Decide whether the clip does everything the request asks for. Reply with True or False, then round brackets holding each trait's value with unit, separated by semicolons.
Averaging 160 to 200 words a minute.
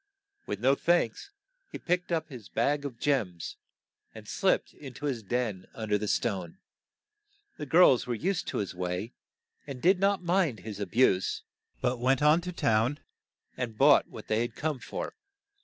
True (175 wpm)